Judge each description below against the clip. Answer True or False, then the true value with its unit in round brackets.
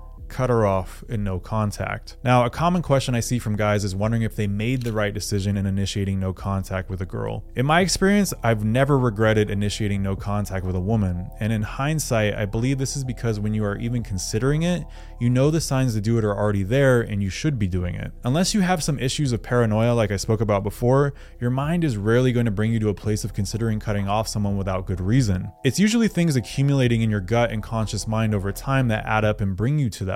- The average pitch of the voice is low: True (110 Hz)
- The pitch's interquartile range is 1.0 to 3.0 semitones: False (4.0 semitones)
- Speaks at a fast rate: True (245 wpm)